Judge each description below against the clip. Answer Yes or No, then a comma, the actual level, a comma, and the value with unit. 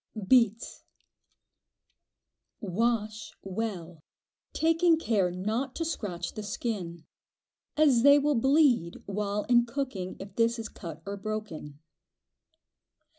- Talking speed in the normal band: No, slow, 105 wpm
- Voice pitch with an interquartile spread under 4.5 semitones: No, average, 4.9 semitones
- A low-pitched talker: No, high, 215 Hz